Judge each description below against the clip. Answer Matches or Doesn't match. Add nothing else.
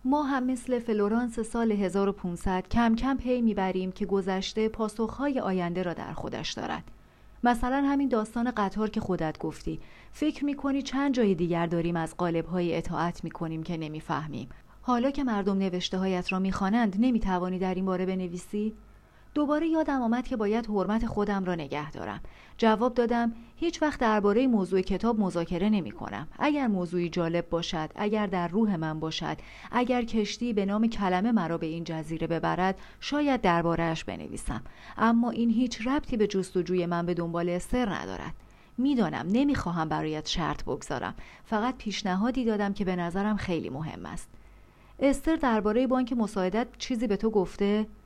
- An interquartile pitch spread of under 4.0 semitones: Doesn't match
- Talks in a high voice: Matches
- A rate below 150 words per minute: Doesn't match